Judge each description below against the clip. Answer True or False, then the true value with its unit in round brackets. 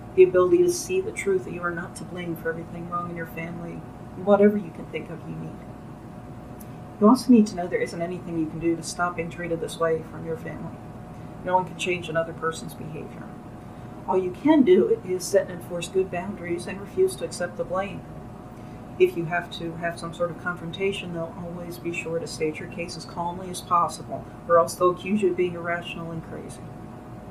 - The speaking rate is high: True (220 wpm)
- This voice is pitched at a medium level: True (175 Hz)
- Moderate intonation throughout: False (1.9 semitones)